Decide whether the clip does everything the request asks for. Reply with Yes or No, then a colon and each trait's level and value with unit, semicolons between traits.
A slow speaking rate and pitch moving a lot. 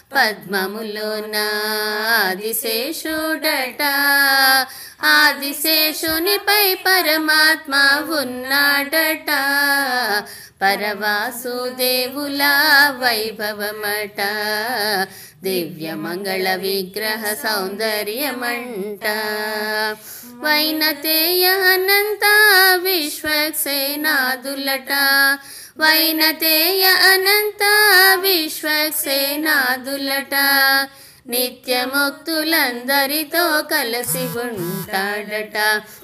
Yes: slow, 30 wpm; wide, 6.5 semitones